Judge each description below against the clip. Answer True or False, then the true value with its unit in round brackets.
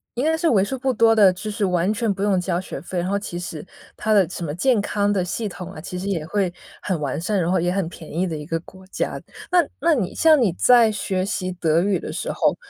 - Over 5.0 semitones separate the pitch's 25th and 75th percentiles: False (3.4 semitones)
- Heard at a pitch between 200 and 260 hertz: False (190 Hz)